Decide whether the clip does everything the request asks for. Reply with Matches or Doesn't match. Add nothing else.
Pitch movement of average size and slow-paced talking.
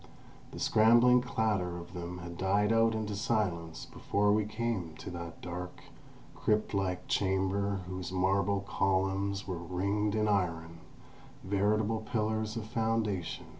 Matches